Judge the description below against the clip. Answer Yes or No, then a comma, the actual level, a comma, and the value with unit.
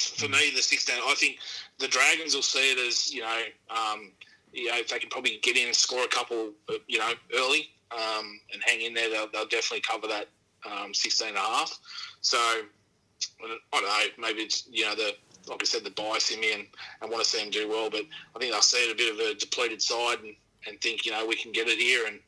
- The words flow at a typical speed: No, fast, 250 wpm